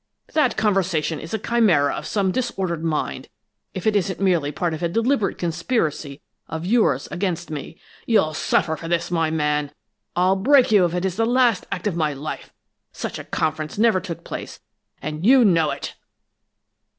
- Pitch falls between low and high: Yes, medium, 175 Hz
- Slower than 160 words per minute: No, average, 175 wpm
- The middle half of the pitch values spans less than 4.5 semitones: No, average, 4.9 semitones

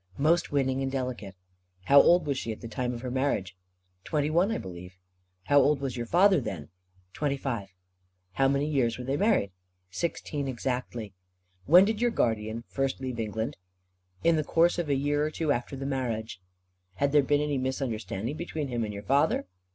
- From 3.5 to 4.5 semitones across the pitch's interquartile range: Yes, average, 4.1 semitones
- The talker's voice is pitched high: No, low, 135 Hz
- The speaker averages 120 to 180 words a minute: No, average, 190 wpm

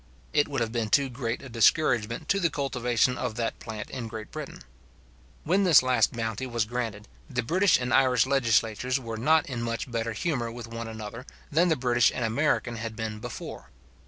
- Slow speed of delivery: No, average, 190 wpm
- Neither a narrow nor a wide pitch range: Yes, average, 3.0 semitones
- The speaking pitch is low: Yes, low, 120 Hz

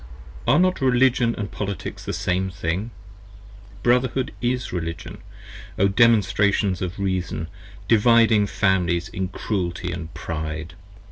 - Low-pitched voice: Yes, low, 100 Hz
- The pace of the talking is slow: Yes, slow, 120 wpm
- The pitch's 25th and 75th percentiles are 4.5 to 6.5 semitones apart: Yes, average, 4.8 semitones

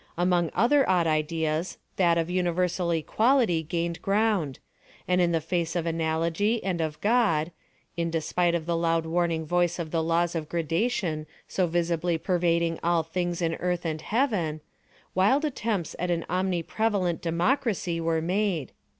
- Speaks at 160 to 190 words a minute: No, average, 150 wpm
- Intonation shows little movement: Yes, narrow, 2.0 semitones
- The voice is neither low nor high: Yes, medium, 170 Hz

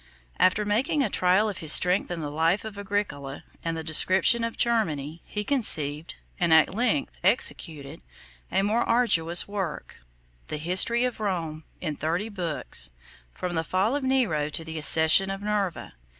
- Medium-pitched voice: Yes, medium, 180 Hz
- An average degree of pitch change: Yes, average, 4.9 semitones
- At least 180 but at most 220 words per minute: No, average, 165 wpm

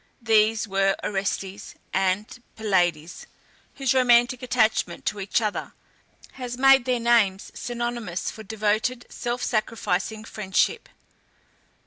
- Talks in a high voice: Yes, high, 220 Hz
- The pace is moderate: No, slow, 105 wpm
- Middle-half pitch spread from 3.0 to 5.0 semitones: Yes, average, 3.6 semitones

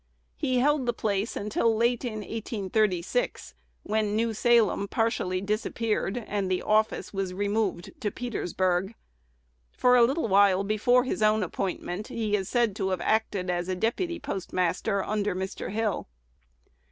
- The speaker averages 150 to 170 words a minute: No, average, 140 wpm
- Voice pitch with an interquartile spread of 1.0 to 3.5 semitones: Yes, average, 3.1 semitones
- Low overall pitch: No, high, 210 Hz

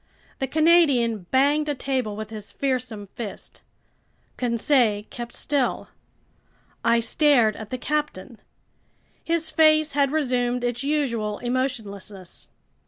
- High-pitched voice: Yes, very high, 250 Hz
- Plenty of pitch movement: No, average, 4.6 semitones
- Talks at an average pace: No, slow, 110 wpm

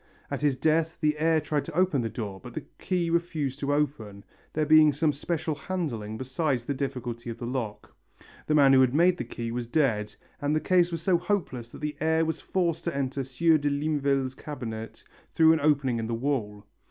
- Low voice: No, medium, 145 Hz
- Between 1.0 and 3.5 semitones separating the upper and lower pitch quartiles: No, average, 4.4 semitones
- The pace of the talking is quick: Yes, fast, 210 wpm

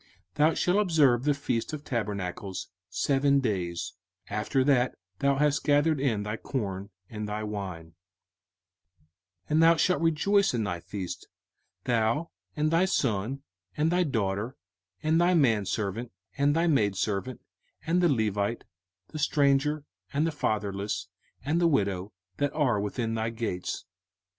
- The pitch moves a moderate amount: No, wide, 6.4 semitones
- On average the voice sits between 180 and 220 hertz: No, low, 125 Hz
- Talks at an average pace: Yes, average, 145 wpm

